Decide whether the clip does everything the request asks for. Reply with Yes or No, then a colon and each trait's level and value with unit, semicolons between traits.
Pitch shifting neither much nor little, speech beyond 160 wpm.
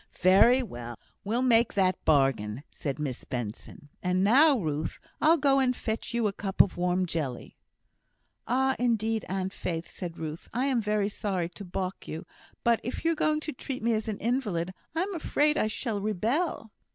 No: wide, 6.2 semitones; average, 180 wpm